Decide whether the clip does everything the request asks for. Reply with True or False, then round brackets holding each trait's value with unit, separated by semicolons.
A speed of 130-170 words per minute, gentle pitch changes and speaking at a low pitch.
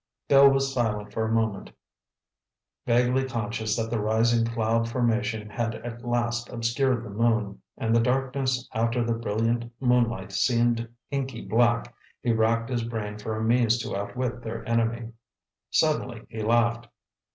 True (150 wpm; 1.3 semitones; 115 Hz)